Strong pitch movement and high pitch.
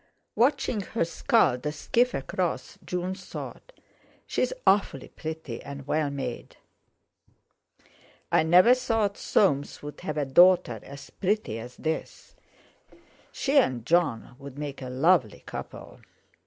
No: wide, 6.3 semitones; medium, 160 Hz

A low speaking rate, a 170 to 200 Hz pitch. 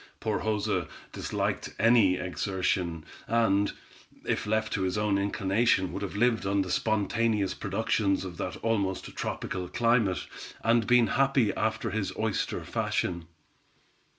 No: slow, 130 wpm; low, 105 Hz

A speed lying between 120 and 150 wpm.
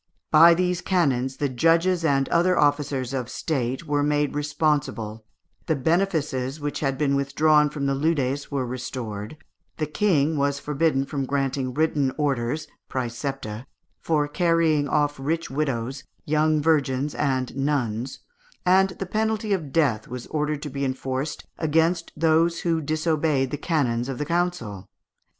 Yes: average, 145 wpm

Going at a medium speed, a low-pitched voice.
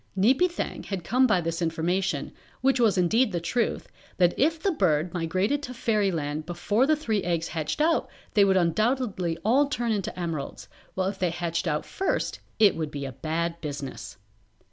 No: average, 180 wpm; medium, 185 Hz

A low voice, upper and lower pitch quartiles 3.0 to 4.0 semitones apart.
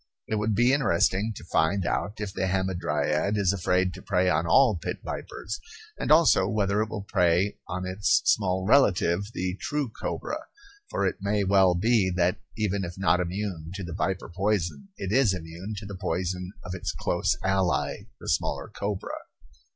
No: very low, 95 Hz; narrow, 2.5 semitones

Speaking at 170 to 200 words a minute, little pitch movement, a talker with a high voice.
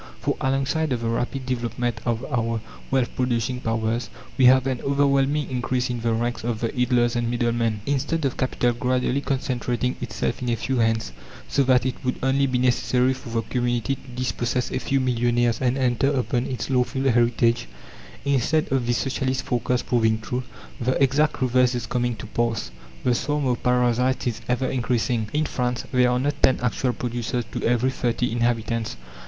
No: average, 180 wpm; narrow, 1.7 semitones; low, 125 Hz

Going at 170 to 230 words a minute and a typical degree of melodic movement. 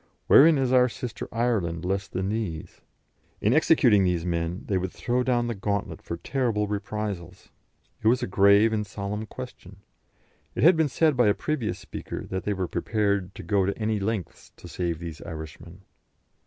Yes: average, 180 wpm; average, 4.4 semitones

